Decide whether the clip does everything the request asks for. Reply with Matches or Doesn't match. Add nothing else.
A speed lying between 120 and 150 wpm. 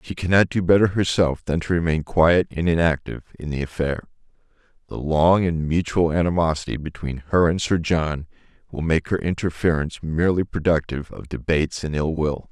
Doesn't match